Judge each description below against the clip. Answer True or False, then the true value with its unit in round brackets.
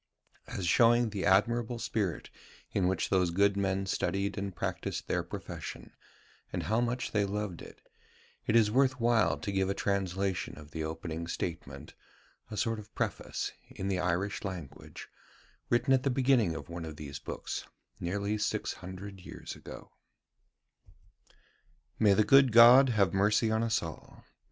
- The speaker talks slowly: False (155 wpm)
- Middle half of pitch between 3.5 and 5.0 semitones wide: True (3.8 semitones)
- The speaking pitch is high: False (100 Hz)